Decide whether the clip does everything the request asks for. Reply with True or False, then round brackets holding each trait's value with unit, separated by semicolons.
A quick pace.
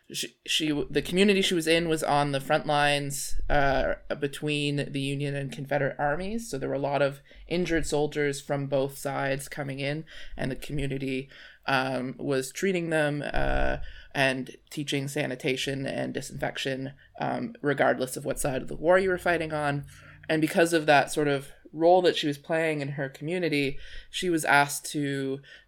False (175 wpm)